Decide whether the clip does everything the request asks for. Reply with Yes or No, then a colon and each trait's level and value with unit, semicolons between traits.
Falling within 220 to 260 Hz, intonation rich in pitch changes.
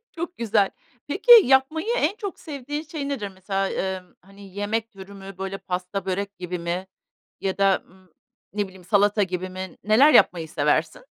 No: high, 200 Hz; wide, 5.8 semitones